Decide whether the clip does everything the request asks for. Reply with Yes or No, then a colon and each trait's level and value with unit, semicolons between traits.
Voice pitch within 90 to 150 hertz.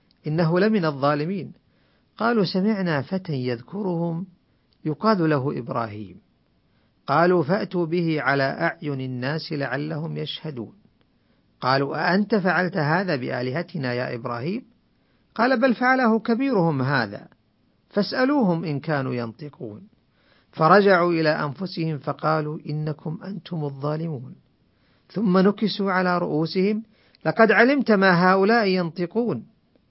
No: medium, 170 Hz